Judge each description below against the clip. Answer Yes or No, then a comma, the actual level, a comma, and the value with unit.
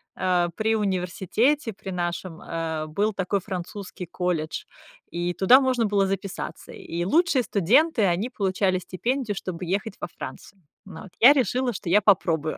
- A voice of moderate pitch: No, high, 195 Hz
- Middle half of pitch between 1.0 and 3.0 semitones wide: No, average, 3.9 semitones